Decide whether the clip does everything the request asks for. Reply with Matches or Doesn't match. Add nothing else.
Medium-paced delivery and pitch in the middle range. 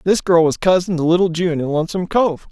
Doesn't match